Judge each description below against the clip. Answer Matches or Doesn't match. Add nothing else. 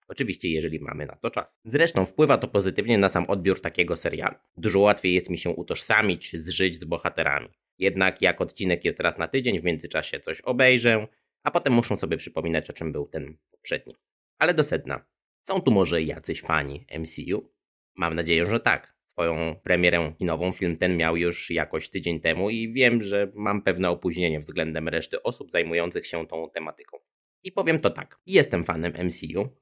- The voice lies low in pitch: Matches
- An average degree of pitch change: Matches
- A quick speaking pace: Matches